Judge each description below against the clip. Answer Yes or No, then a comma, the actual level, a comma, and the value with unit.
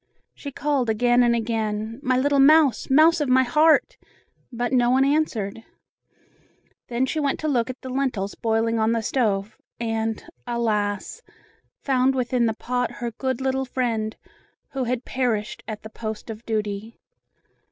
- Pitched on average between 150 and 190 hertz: No, high, 240 Hz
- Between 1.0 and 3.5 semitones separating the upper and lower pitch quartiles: Yes, average, 3.1 semitones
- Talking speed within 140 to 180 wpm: Yes, average, 155 wpm